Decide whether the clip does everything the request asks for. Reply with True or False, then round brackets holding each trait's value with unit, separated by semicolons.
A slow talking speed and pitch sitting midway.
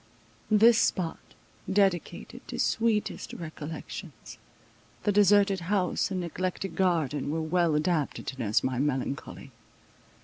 True (110 wpm; 175 Hz)